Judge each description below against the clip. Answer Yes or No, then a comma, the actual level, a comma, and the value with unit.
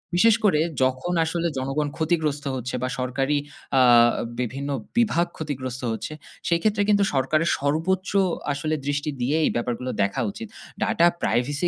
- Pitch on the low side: No, medium, 145 Hz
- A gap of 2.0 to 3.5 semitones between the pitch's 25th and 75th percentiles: No, average, 4.7 semitones